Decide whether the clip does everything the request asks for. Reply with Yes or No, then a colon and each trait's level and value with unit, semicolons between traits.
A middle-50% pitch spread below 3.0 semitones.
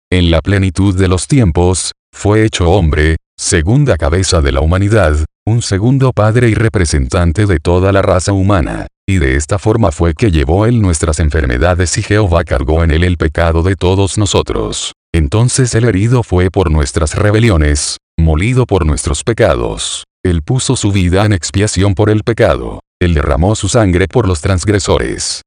No: average, 4.1 semitones